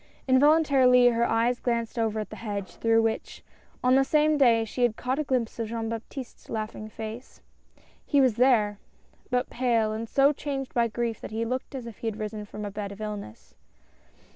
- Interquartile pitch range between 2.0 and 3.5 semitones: Yes, average, 2.8 semitones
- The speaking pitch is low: No, high, 230 Hz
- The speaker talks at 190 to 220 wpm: Yes, average, 195 wpm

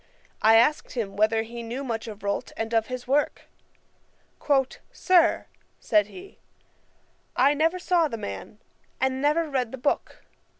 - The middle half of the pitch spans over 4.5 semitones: Yes, average, 4.9 semitones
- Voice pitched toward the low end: No, high, 245 Hz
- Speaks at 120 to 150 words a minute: Yes, average, 145 wpm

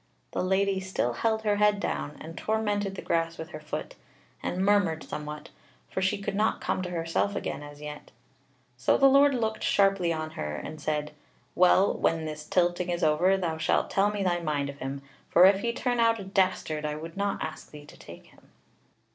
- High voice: No, medium, 180 Hz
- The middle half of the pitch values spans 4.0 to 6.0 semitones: Yes, average, 4.6 semitones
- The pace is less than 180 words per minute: No, fast, 205 wpm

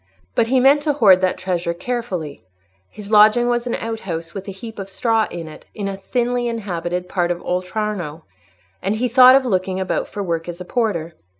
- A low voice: No, high, 195 Hz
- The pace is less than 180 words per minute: No, average, 200 wpm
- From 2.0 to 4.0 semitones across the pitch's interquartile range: No, average, 4.9 semitones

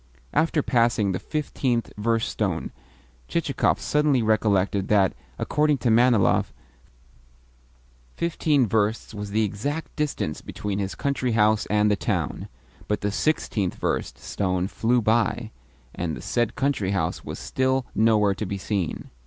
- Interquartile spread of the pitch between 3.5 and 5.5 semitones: Yes, average, 4.4 semitones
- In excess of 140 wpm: No, slow, 135 wpm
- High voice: No, low, 110 Hz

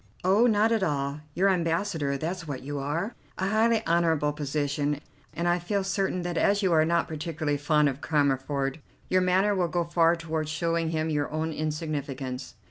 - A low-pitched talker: No, medium, 160 Hz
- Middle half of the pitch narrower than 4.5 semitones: Yes, average, 3.6 semitones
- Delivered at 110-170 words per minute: No, average, 180 wpm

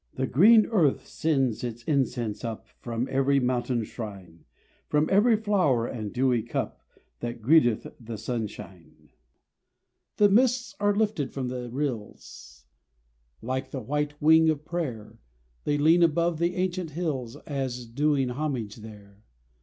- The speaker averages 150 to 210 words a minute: No, slow, 135 wpm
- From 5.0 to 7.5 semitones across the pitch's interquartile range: Yes, wide, 5.5 semitones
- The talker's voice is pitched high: No, low, 135 Hz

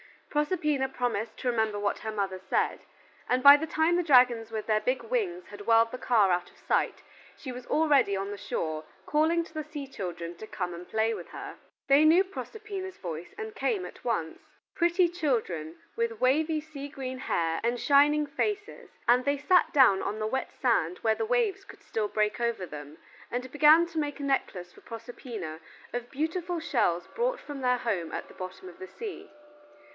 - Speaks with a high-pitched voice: Yes, very high, 255 Hz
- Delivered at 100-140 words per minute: No, average, 195 wpm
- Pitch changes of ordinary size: No, wide, 7.0 semitones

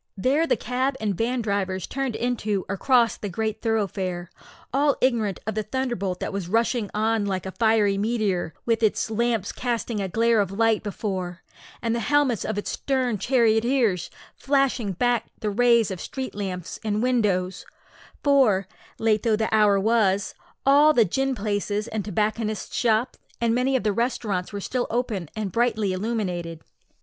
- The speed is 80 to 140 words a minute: No, average, 165 wpm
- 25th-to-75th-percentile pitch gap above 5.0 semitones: No, average, 3.4 semitones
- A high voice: Yes, high, 220 Hz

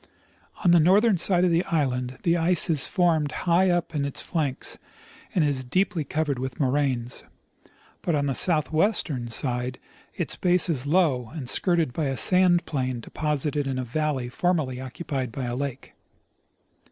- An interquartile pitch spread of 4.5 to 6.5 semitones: Yes, average, 5.0 semitones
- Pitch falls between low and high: Yes, medium, 150 Hz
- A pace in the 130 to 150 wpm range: No, average, 165 wpm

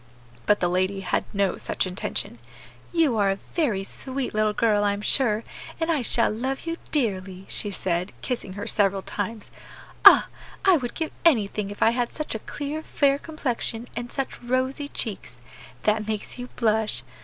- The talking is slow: No, average, 175 wpm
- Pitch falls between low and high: No, high, 225 Hz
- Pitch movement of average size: Yes, average, 4.9 semitones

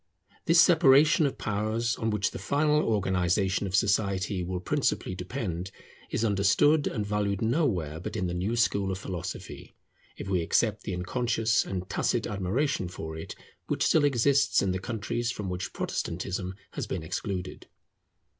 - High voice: No, low, 100 Hz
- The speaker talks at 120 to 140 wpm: No, average, 155 wpm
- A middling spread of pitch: Yes, average, 4.4 semitones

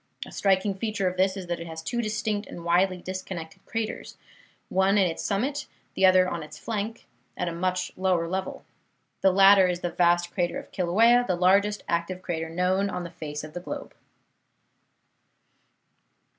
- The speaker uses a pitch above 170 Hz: Yes, medium, 185 Hz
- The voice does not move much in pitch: Yes, narrow, 2.3 semitones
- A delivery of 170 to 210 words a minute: Yes, average, 175 wpm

